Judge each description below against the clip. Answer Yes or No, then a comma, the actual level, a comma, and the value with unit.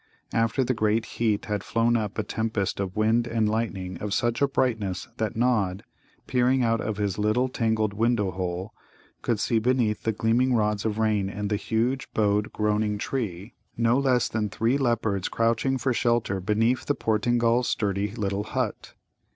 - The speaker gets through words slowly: No, average, 170 wpm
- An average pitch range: No, narrow, 2.3 semitones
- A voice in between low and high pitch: No, low, 110 Hz